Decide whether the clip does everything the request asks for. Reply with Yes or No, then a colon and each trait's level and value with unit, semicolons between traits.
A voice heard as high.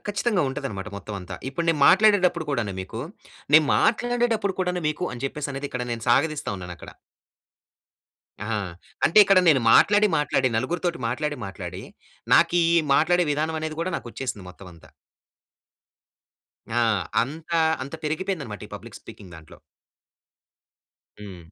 No: medium, 150 Hz